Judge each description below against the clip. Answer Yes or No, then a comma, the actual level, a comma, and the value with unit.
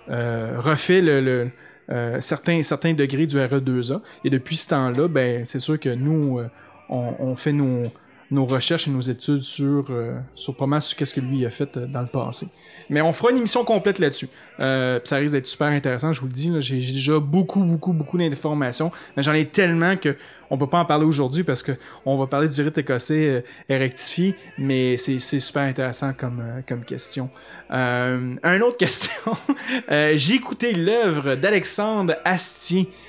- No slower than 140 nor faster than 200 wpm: Yes, average, 195 wpm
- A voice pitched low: No, medium, 145 Hz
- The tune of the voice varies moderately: Yes, average, 4.2 semitones